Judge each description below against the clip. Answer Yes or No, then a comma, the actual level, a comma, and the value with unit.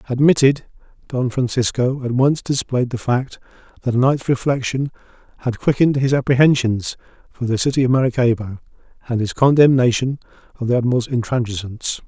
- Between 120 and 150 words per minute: Yes, average, 140 wpm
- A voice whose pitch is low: Yes, low, 125 Hz